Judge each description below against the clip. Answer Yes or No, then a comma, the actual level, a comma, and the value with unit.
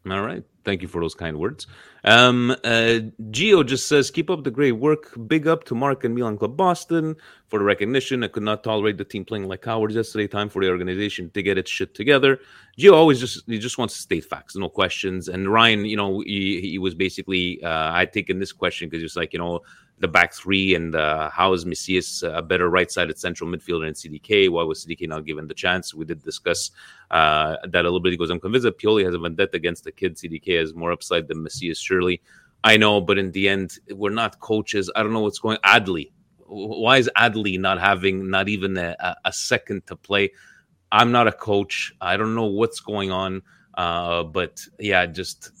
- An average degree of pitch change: Yes, average, 4.0 semitones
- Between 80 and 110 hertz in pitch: Yes, low, 100 Hz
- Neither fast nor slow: No, fast, 220 wpm